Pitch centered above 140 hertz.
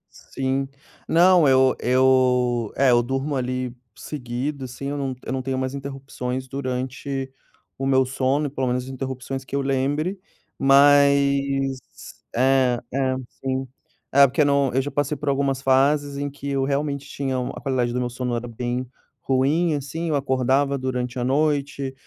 No: low, 135 Hz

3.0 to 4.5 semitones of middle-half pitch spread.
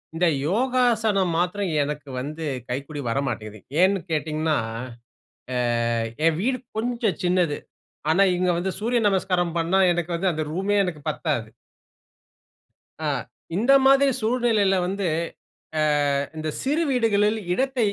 No: wide, 5.6 semitones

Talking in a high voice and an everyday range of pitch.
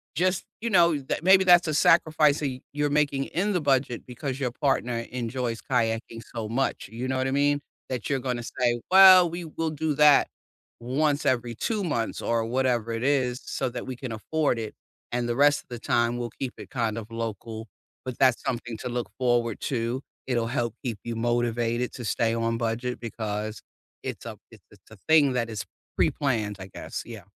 No: low, 125 Hz; average, 3.6 semitones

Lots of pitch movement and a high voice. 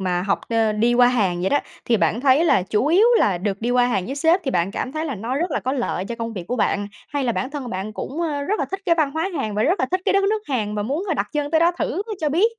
Yes: wide, 6.8 semitones; very high, 255 Hz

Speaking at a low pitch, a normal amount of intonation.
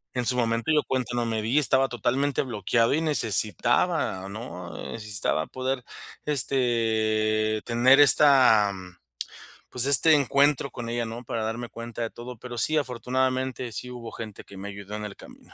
Yes: low, 120 Hz; average, 3.0 semitones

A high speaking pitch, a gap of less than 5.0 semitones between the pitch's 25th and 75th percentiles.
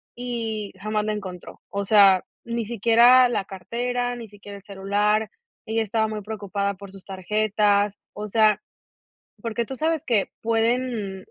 Yes: high, 215 Hz; narrow, 2.5 semitones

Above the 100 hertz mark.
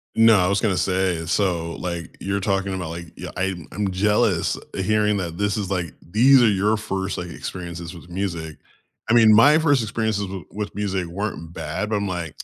No: very low, 95 Hz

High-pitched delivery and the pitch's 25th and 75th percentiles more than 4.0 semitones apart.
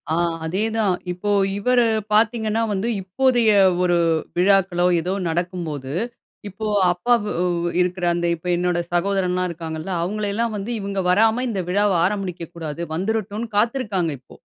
No: high, 195 Hz; average, 3.5 semitones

